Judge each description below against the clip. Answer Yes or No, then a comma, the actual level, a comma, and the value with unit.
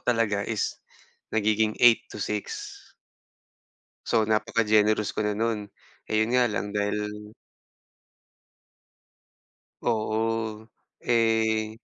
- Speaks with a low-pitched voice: Yes, low, 110 Hz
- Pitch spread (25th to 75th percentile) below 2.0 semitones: Yes, narrow, 1.2 semitones